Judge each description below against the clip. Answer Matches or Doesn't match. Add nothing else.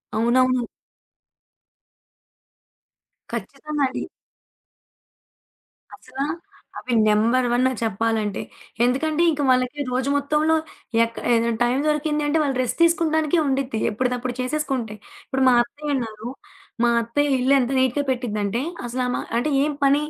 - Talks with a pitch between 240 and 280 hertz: Matches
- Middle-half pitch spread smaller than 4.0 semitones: Matches